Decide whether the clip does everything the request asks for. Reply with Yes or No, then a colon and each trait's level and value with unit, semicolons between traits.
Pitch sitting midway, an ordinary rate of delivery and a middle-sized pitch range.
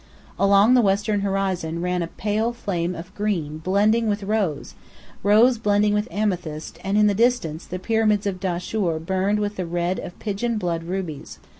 No: high, 195 Hz; average, 170 wpm; average, 3.0 semitones